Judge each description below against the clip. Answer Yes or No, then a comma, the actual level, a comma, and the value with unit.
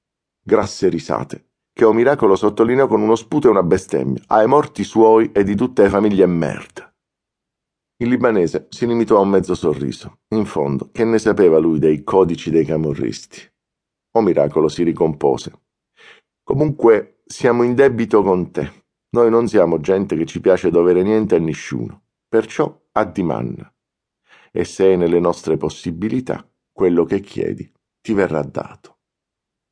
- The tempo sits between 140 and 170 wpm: Yes, average, 155 wpm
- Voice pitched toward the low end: Yes, low, 105 Hz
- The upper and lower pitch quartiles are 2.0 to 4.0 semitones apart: No, average, 5.0 semitones